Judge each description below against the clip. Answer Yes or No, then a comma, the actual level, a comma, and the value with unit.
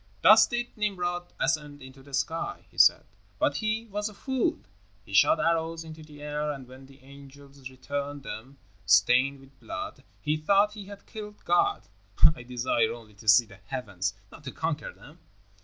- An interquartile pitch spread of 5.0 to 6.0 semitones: Yes, average, 5.3 semitones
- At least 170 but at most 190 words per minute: Yes, average, 175 wpm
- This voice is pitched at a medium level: Yes, medium, 145 Hz